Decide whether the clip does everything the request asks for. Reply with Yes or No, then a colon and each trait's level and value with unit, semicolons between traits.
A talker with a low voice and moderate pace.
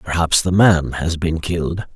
Yes: very low, 85 Hz; average, 185 wpm